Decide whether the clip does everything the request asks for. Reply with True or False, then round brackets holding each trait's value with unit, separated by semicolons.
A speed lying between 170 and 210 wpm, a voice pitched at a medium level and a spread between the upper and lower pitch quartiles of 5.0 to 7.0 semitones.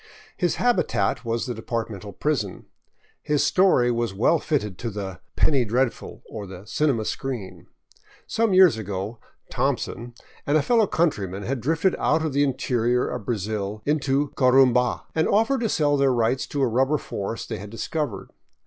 False (175 wpm; 125 Hz; 5.4 semitones)